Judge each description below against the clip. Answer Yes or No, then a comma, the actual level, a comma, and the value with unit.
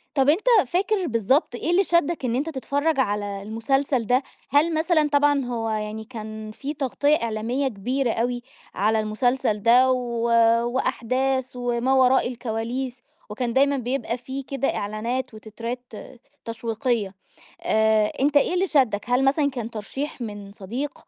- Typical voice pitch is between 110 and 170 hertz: No, very high, 250 Hz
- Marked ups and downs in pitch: No, average, 3.7 semitones